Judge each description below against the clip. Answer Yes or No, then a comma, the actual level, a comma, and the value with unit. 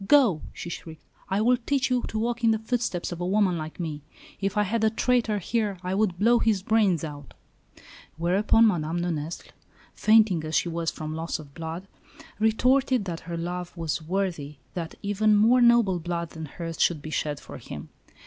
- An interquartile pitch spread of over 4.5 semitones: Yes, average, 5.0 semitones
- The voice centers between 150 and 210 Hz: Yes, medium, 185 Hz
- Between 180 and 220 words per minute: Yes, average, 195 wpm